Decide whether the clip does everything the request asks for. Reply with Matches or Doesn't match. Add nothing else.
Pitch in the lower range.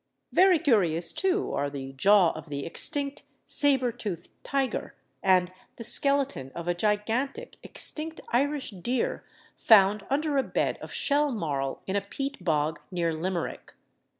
Doesn't match